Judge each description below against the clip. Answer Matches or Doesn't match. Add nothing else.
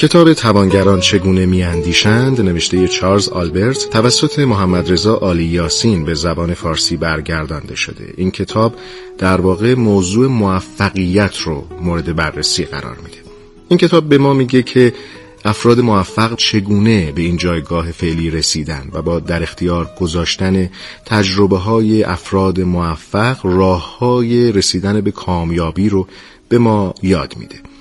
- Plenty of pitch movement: Doesn't match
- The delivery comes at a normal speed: Matches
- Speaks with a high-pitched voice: Doesn't match